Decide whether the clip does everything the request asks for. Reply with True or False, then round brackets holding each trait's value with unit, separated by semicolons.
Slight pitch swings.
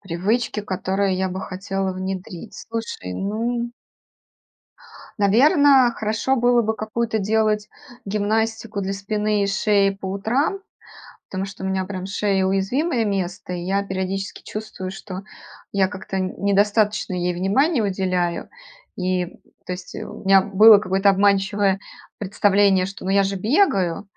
True (2.2 semitones)